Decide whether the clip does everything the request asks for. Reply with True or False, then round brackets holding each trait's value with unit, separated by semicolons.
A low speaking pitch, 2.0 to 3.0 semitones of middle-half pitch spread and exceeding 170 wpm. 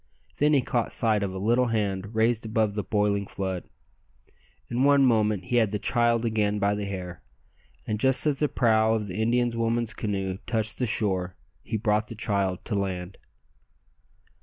True (110 Hz; 2.7 semitones; 180 wpm)